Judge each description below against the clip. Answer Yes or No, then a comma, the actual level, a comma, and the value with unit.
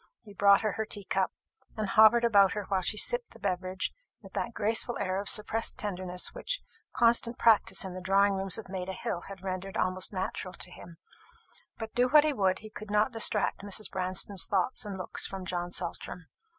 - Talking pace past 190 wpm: Yes, average, 200 wpm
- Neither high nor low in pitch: No, high, 200 Hz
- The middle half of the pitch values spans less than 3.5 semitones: Yes, average, 2.7 semitones